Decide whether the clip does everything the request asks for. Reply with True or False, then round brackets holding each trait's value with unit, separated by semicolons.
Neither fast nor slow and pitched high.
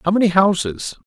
False (170 wpm; 180 Hz)